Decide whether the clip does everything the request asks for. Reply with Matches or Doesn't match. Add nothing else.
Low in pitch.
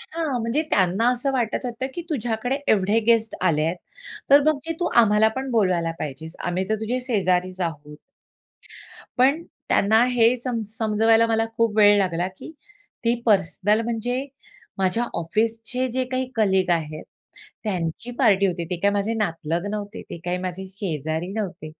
Doesn't match